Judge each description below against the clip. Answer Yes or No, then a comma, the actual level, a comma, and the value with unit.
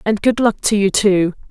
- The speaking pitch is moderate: No, high, 205 Hz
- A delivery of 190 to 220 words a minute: No, fast, 240 wpm